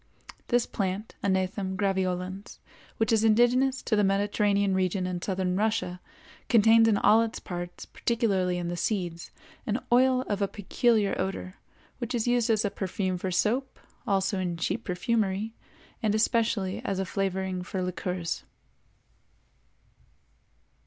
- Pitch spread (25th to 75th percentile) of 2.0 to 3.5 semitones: Yes, average, 3.2 semitones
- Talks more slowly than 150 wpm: Yes, average, 140 wpm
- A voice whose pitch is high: Yes, high, 200 Hz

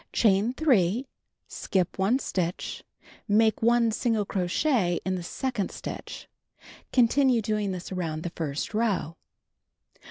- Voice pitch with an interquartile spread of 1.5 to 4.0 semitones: No, average, 4.6 semitones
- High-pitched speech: Yes, high, 205 Hz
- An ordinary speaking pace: No, slow, 120 wpm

